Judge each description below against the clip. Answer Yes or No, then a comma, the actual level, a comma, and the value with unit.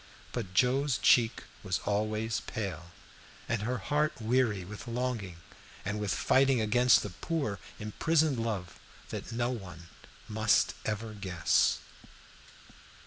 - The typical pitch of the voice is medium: No, low, 110 Hz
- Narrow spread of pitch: No, average, 3.6 semitones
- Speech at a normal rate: No, slow, 120 wpm